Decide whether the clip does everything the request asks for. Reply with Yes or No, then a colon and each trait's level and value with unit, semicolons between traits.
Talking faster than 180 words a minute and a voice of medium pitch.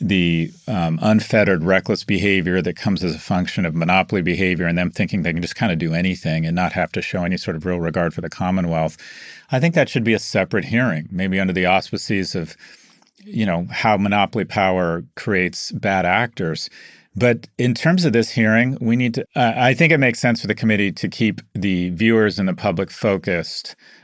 No: fast, 205 wpm; very low, 95 Hz